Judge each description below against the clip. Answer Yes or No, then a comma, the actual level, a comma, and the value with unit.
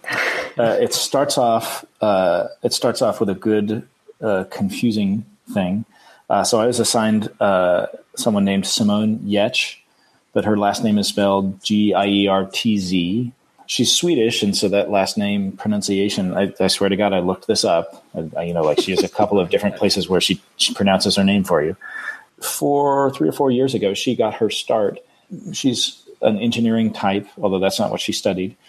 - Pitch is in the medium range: No, low, 105 Hz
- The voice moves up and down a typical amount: Yes, average, 3.9 semitones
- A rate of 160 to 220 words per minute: Yes, average, 195 wpm